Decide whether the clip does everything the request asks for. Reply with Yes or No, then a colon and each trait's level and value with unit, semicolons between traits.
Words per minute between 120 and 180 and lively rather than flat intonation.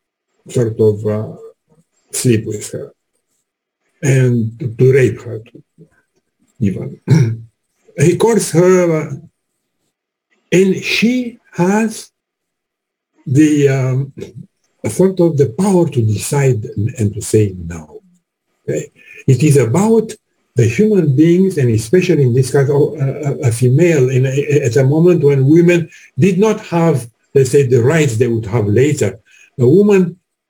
Yes: average, 140 wpm; wide, 6.0 semitones